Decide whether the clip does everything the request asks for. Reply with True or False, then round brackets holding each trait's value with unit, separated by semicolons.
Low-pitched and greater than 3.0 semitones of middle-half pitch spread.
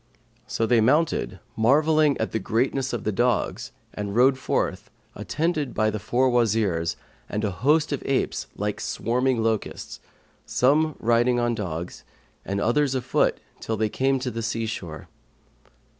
True (120 Hz; 3.6 semitones)